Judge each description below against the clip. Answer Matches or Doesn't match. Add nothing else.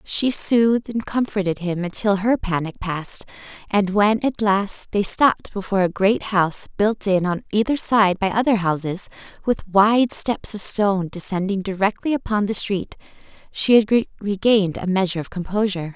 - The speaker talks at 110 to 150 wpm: Doesn't match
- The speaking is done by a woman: Matches